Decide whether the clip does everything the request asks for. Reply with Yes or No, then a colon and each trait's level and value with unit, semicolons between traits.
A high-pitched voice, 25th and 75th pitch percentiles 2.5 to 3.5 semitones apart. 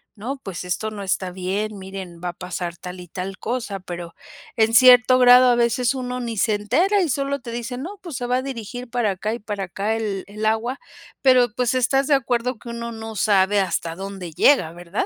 No: high, 220 Hz; average, 4.5 semitones